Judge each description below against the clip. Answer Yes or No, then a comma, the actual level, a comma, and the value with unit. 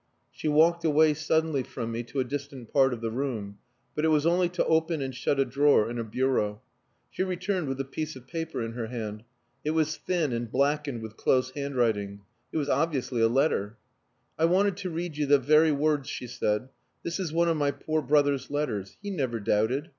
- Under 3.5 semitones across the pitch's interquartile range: No, average, 4.8 semitones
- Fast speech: Yes, fast, 210 wpm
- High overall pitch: No, medium, 140 Hz